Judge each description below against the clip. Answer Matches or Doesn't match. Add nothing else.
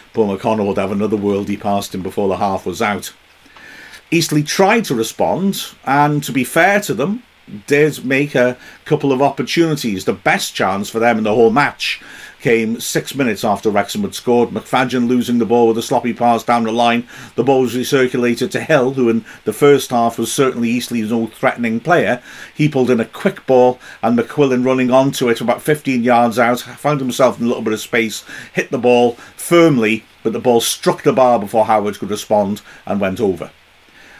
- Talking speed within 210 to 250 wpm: Doesn't match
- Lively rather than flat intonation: Doesn't match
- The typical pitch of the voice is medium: Doesn't match